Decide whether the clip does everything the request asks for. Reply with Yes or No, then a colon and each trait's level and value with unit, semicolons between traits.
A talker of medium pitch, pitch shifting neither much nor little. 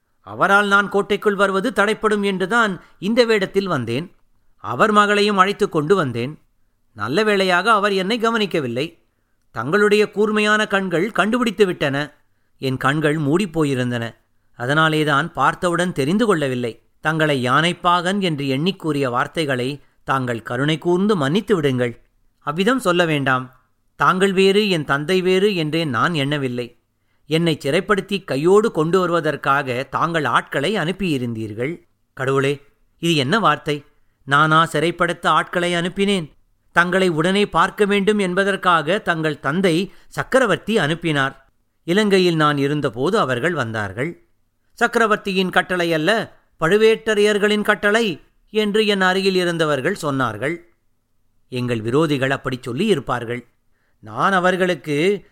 No: medium, 160 Hz; wide, 6.8 semitones